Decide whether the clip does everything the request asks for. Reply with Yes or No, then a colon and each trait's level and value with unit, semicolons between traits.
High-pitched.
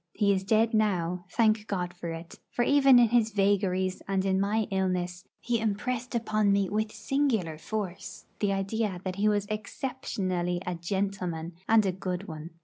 Yes: high, 200 Hz